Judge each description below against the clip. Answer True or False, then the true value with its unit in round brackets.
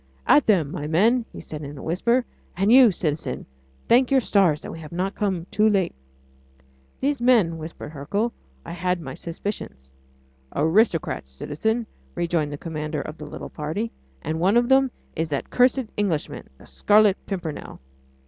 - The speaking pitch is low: False (180 Hz)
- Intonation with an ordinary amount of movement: False (6.2 semitones)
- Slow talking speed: False (165 wpm)